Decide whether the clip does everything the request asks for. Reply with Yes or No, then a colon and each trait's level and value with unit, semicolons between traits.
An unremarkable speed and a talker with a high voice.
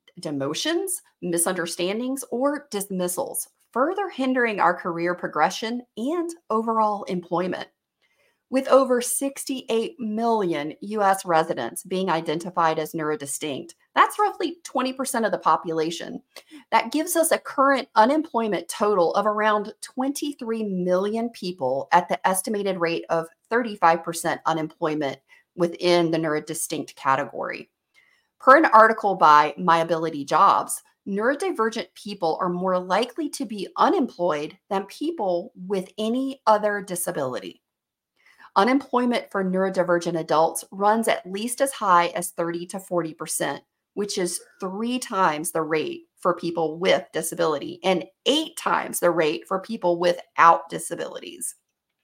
No: slow, 120 wpm; high, 195 Hz